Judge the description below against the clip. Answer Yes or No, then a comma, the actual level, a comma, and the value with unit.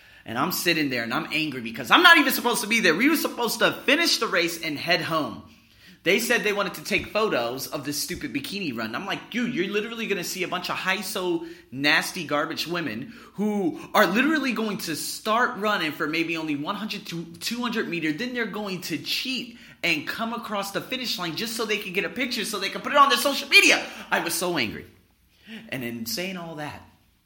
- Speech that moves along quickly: Yes, fast, 230 wpm